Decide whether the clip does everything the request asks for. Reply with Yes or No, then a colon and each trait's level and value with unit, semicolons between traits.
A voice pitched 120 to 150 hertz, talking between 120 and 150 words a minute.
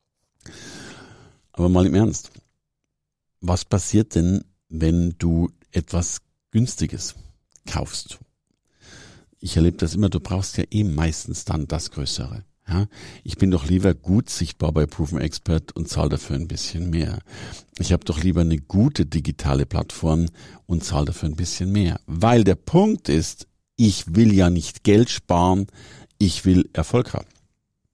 No: very low, 90 Hz; average, 145 wpm